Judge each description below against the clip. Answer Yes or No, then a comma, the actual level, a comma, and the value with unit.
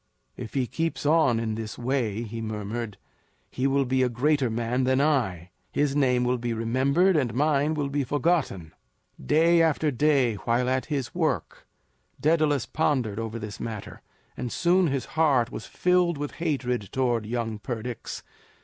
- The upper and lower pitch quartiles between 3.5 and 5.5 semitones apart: Yes, average, 4.3 semitones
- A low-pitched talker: Yes, low, 130 Hz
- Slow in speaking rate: No, average, 160 wpm